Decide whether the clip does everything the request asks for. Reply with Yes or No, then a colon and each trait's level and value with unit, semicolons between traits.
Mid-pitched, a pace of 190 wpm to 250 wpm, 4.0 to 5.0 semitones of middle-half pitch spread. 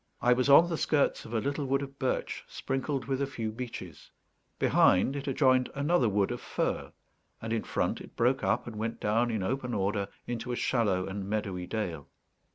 No: low, 120 Hz; average, 195 wpm; average, 4.3 semitones